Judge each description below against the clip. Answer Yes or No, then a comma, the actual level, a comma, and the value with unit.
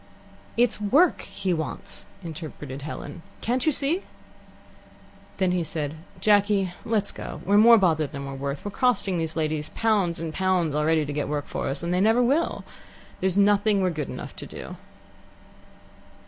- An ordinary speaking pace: Yes, average, 165 wpm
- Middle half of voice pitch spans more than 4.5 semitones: Yes, average, 5.2 semitones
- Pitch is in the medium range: Yes, medium, 180 Hz